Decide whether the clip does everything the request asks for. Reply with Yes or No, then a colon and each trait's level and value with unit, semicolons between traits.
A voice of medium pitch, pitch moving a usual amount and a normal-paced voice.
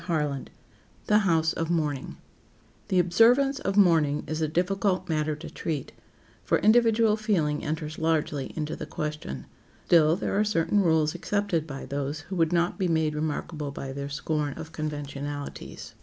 Yes: medium, 160 Hz; average, 3.5 semitones; average, 160 wpm